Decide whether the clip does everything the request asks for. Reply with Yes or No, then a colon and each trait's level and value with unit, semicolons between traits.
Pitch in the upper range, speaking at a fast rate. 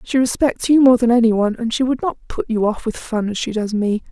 Yes: high, 235 Hz; fast, 290 wpm